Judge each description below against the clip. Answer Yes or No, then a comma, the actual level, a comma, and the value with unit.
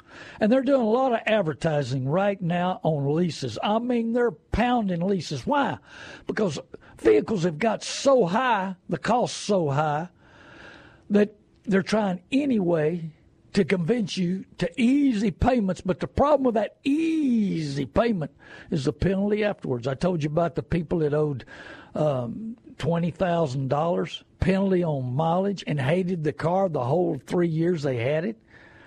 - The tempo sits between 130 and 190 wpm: Yes, average, 155 wpm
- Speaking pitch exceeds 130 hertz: Yes, medium, 185 Hz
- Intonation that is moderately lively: No, wide, 6.0 semitones